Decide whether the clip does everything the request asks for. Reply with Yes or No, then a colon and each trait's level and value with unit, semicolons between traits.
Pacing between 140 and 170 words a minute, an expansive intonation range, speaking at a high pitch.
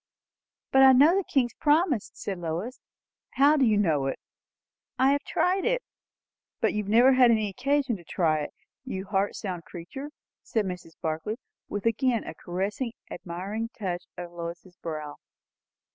Yes: average, 160 wpm; wide, 7.0 semitones; high, 210 Hz